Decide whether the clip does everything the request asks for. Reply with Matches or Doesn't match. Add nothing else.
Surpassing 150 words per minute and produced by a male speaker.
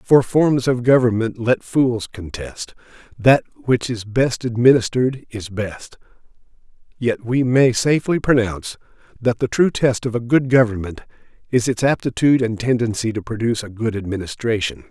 Doesn't match